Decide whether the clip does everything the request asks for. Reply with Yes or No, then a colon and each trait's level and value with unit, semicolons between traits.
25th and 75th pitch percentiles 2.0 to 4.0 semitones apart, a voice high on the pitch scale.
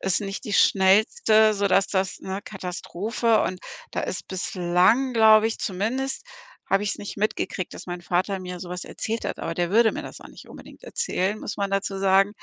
Yes: average, 2.8 semitones; high, 195 Hz